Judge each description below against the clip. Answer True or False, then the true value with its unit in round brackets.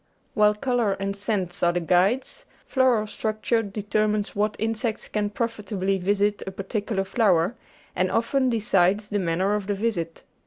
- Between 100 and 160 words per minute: True (155 wpm)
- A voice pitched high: True (205 Hz)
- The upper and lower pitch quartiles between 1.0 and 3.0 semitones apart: True (2.5 semitones)